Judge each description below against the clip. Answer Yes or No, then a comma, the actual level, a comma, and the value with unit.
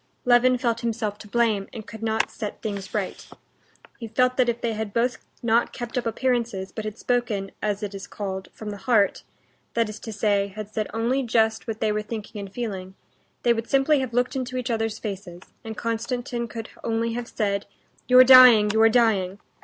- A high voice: Yes, high, 225 Hz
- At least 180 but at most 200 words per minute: Yes, average, 195 wpm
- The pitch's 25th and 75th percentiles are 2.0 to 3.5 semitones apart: Yes, narrow, 2.5 semitones